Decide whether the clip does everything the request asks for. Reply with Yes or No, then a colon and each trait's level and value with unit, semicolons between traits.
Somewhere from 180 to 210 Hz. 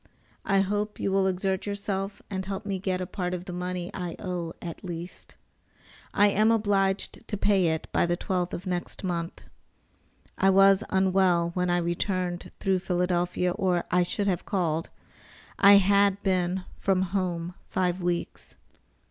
Yes: medium, 185 Hz